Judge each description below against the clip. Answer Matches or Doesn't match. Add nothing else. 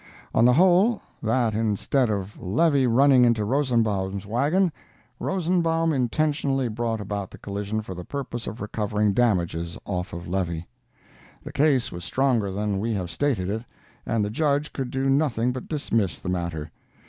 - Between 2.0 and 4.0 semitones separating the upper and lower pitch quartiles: Doesn't match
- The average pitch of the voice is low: Matches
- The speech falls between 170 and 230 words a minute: Doesn't match